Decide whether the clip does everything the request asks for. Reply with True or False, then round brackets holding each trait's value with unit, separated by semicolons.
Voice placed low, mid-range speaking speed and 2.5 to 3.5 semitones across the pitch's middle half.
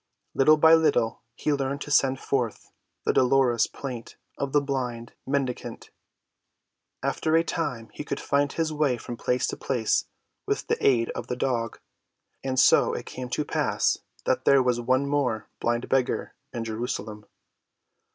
True (130 Hz; 160 wpm; 2.9 semitones)